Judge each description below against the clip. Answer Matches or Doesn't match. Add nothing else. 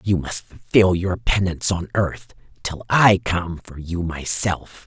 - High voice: Doesn't match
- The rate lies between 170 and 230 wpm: Doesn't match